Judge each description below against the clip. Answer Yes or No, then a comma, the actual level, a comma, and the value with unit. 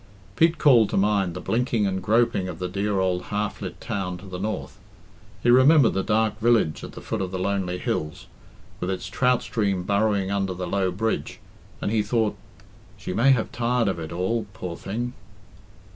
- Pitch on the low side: Yes, low, 100 Hz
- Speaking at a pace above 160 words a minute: Yes, average, 190 wpm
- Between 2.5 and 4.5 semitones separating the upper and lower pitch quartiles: Yes, average, 3.6 semitones